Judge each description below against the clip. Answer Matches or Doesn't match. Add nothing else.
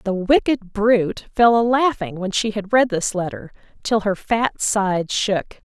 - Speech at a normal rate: Matches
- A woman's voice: Matches